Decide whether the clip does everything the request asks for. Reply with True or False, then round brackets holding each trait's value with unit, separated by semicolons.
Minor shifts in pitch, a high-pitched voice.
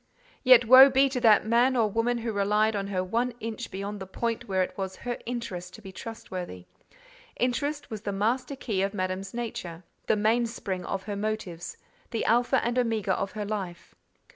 False (3.8 semitones; 215 Hz)